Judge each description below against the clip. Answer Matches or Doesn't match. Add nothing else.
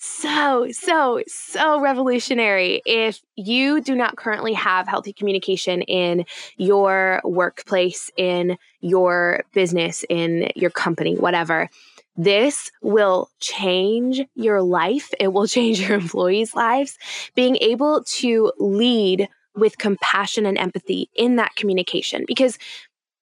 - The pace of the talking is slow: Matches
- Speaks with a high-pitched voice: Matches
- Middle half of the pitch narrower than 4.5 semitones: Doesn't match